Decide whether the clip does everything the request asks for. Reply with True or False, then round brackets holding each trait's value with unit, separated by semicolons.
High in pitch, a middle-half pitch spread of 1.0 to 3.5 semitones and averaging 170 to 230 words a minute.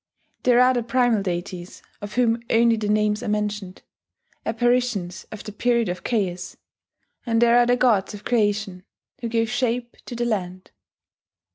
False (225 Hz; 3.0 semitones; 160 wpm)